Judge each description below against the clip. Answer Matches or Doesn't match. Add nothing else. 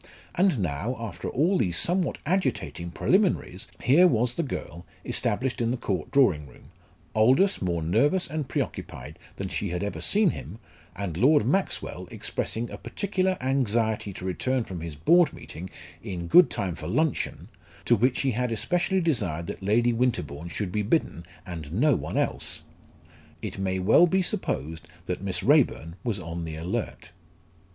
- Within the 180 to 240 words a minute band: Doesn't match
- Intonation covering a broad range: Matches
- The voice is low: Matches